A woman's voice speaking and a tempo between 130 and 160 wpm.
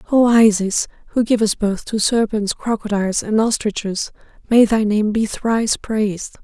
Yes: female; average, 150 wpm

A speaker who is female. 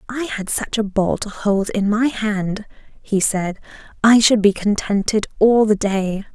Yes: female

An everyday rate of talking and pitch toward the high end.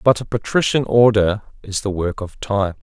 No: average, 190 wpm; low, 105 Hz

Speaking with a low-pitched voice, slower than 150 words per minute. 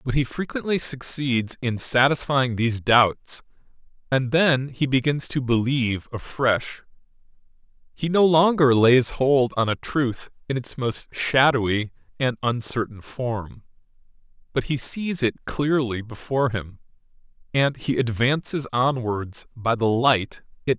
Yes: low, 130 Hz; slow, 135 wpm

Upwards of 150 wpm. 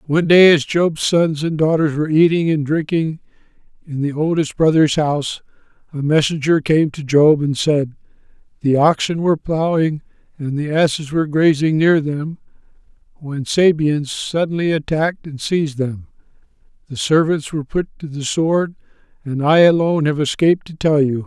Yes: average, 160 wpm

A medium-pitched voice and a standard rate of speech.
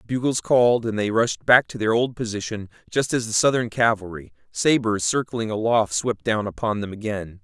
No: low, 110 Hz; average, 185 wpm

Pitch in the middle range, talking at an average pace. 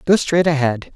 Yes: medium, 150 Hz; average, 190 wpm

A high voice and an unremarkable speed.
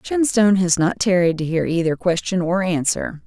No: medium, 180 Hz; average, 185 wpm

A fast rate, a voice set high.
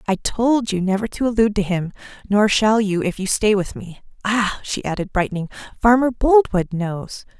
No: average, 185 wpm; high, 205 Hz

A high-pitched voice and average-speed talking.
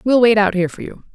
No: high, 205 Hz; fast, 315 wpm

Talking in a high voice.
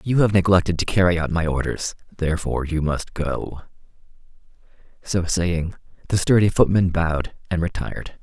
No: very low, 85 Hz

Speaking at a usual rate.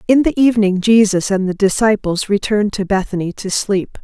Yes: average, 180 wpm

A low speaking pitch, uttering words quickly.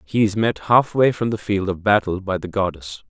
Yes: low, 100 Hz; fast, 230 wpm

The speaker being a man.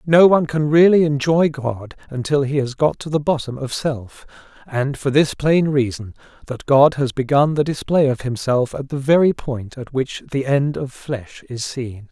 Yes: male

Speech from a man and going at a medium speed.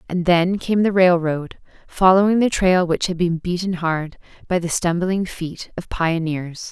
No: female; average, 170 wpm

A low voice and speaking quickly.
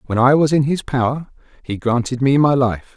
Yes: low, 130 Hz; fast, 225 wpm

